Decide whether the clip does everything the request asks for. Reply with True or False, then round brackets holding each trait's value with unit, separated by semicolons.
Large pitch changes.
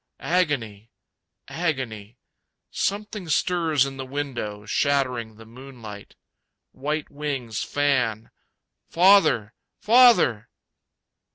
True (5.8 semitones)